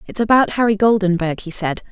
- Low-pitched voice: No, high, 200 Hz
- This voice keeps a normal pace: Yes, average, 190 wpm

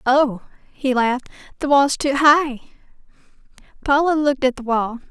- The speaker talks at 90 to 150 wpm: Yes, average, 140 wpm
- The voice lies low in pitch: No, very high, 270 Hz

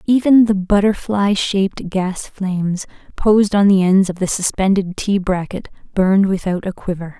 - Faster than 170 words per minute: No, average, 160 wpm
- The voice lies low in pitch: No, high, 195 Hz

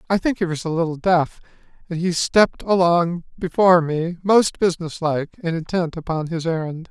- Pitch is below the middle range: No, medium, 170 Hz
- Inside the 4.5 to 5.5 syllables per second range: Yes, 5.4 syllables/s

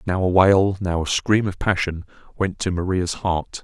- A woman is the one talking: No, male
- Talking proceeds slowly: No, average, 200 wpm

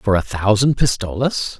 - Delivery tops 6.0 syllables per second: No, 4.5 syllables/s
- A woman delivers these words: No, male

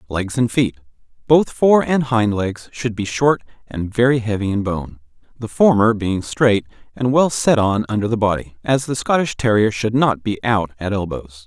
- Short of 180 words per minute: No, average, 190 wpm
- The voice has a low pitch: Yes, low, 110 Hz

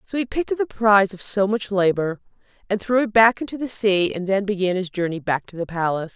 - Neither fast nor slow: No, fast, 255 wpm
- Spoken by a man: No, female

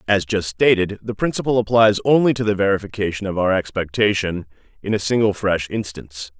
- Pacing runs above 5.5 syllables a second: Yes, 5.8 syllables/s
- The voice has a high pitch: No, low, 100 Hz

